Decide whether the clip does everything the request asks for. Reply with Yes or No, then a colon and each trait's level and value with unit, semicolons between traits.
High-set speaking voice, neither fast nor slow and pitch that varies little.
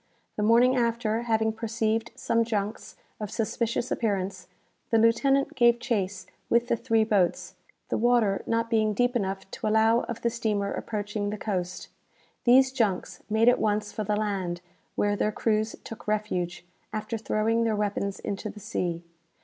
Yes: high, 220 Hz; average, 160 wpm; narrow, 2.0 semitones